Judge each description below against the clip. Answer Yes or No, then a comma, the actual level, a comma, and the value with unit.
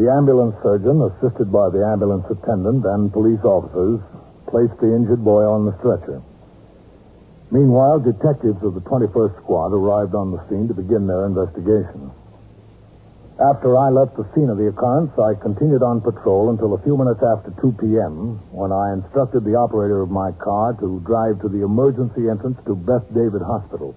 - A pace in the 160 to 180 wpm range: Yes, average, 175 wpm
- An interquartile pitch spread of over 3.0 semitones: Yes, average, 3.4 semitones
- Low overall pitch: Yes, low, 110 Hz